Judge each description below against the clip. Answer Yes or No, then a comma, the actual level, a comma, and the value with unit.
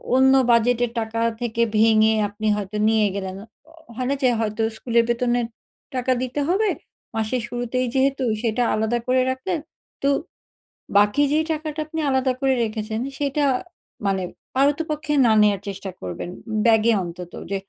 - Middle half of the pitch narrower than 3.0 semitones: No, average, 3.5 semitones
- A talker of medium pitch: No, high, 235 Hz